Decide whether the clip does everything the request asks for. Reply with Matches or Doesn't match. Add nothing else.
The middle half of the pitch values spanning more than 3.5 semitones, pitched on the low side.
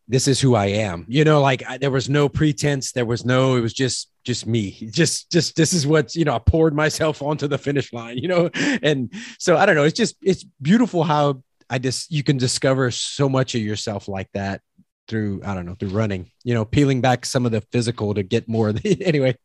Matches